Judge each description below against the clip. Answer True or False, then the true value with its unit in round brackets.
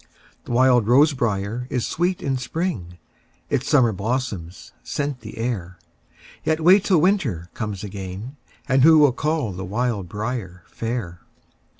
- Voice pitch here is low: True (120 Hz)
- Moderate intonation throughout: False (6.4 semitones)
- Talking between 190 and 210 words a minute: False (140 wpm)